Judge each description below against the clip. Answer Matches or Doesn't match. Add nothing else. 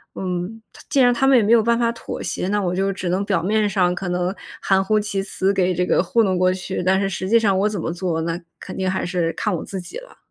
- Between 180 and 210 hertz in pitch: Matches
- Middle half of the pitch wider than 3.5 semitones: Doesn't match